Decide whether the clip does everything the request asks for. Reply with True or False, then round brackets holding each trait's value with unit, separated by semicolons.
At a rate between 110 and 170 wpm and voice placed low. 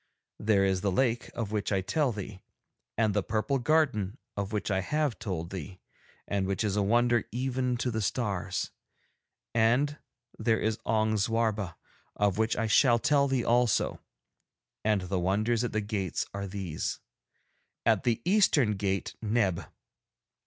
True (155 wpm; 110 Hz)